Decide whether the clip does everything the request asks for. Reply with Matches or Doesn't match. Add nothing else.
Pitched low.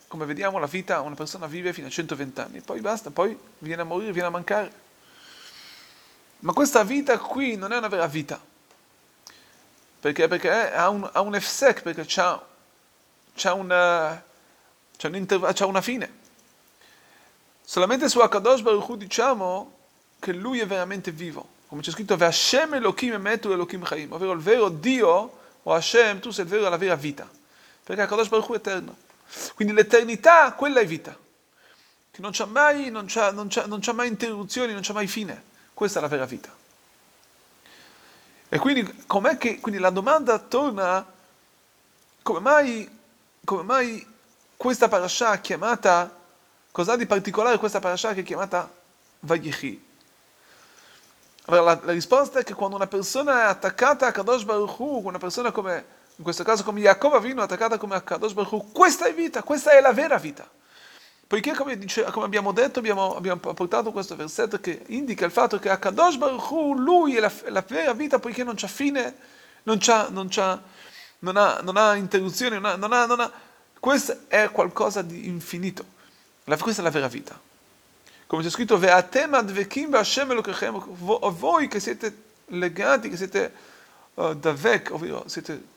Doesn't match